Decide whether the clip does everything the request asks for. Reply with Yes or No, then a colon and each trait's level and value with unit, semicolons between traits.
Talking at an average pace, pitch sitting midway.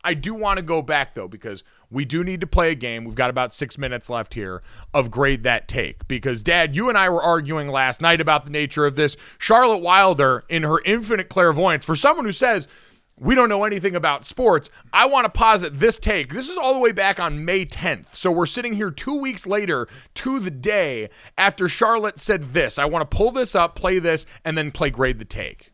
No: fast, 230 wpm; medium, 170 Hz